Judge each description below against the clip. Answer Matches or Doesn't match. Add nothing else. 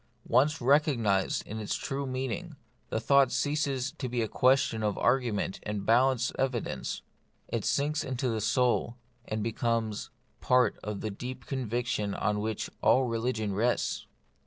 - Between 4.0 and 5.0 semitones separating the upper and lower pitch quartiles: Doesn't match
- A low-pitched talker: Matches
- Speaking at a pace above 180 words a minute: Doesn't match